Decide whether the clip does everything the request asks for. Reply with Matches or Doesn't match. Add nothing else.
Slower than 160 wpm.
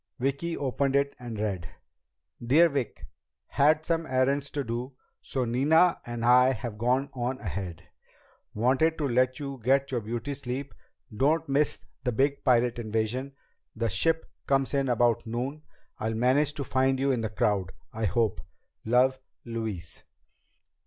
Matches